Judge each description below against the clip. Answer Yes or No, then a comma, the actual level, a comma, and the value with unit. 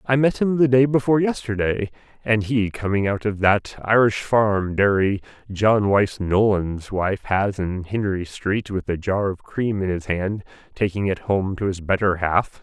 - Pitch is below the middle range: Yes, low, 105 Hz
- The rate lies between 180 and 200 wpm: Yes, average, 185 wpm